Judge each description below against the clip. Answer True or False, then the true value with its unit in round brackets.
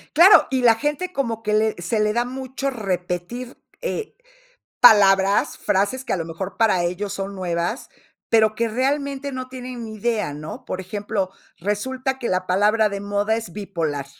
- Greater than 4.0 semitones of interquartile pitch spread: True (4.8 semitones)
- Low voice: False (215 Hz)